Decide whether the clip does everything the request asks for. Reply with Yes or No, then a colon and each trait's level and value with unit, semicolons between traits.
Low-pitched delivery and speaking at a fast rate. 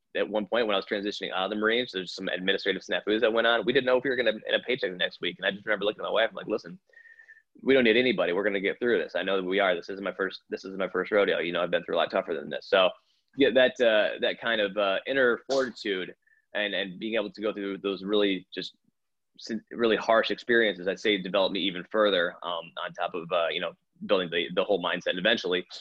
Yes: low, 105 Hz; fast, 280 wpm